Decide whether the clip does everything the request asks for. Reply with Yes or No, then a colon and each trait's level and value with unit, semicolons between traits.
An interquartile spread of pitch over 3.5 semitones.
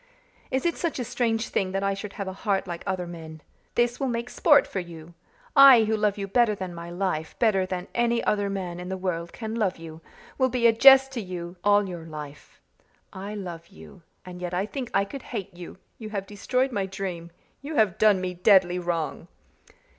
Yes: average, 4.4 semitones